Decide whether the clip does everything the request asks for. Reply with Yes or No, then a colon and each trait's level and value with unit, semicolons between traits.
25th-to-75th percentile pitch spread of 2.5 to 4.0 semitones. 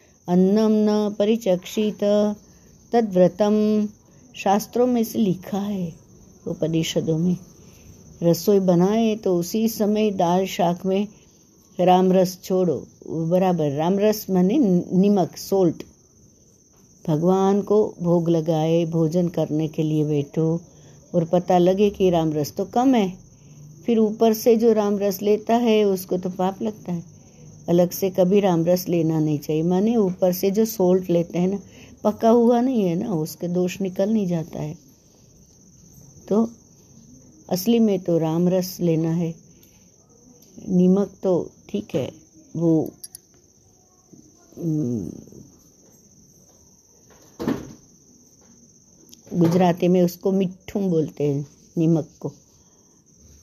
Yes: average, 3.6 semitones